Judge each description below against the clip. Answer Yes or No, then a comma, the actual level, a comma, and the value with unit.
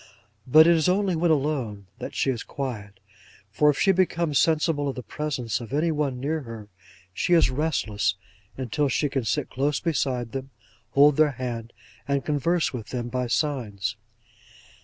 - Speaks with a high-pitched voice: No, medium, 140 Hz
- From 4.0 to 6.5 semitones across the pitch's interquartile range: Yes, average, 4.3 semitones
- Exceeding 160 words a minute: Yes, average, 170 wpm